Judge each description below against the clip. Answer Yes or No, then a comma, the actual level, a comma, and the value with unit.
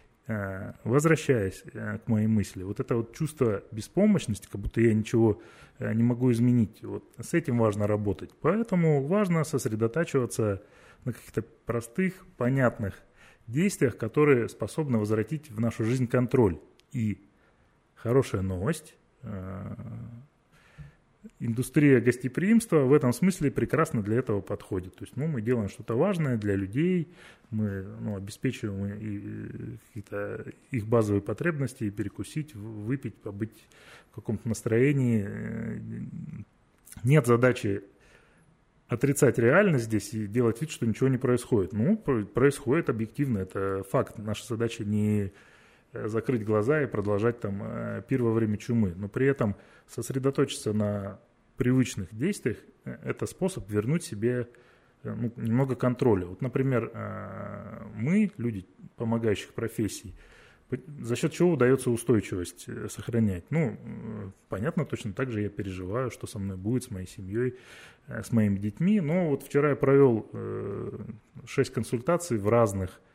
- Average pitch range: Yes, average, 4.3 semitones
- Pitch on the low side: Yes, low, 115 Hz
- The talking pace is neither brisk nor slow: Yes, average, 125 wpm